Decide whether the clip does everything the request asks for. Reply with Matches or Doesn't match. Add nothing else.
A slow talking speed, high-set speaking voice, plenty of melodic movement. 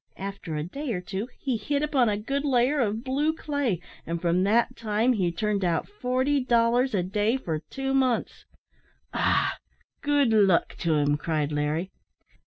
Doesn't match